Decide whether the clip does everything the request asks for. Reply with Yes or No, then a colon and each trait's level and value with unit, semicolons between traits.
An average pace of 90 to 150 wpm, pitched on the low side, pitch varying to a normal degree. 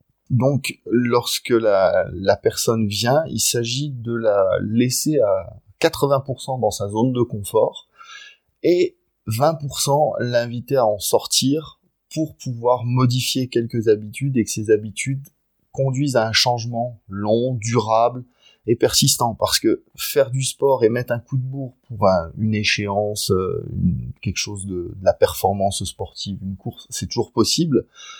Yes: slow, 145 wpm; low, 120 Hz; average, 3.7 semitones